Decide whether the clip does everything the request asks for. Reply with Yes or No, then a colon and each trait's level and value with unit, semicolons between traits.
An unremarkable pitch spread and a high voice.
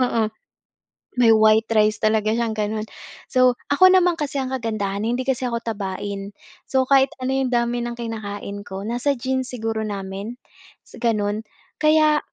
Yes: average, 3.5 semitones; high, 235 Hz